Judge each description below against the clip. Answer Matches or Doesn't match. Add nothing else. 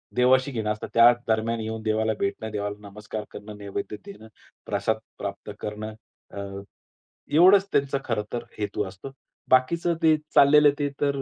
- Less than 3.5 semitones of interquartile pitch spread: Doesn't match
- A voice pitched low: Matches